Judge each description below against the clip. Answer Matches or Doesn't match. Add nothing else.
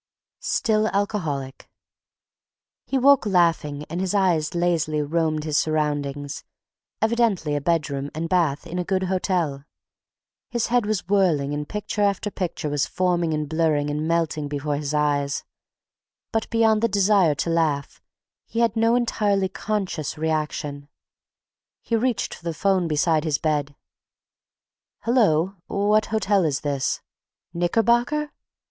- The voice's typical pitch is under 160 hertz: Doesn't match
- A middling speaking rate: Doesn't match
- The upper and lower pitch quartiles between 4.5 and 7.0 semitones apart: Matches